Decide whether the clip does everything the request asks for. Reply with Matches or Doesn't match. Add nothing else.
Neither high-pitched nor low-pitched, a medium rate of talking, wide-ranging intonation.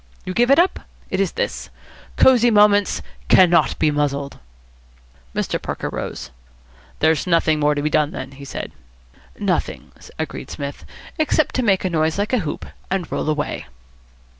Matches